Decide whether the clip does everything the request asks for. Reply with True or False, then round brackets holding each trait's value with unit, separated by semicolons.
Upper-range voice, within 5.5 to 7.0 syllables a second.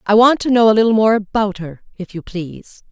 True (210 Hz; 5.7 syllables/s)